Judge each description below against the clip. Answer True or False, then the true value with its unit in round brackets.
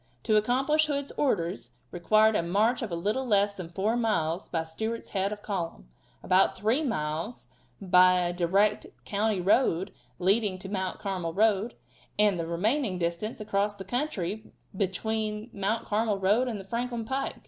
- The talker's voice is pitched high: True (205 Hz)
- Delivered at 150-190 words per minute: True (170 wpm)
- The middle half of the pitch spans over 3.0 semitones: True (3.5 semitones)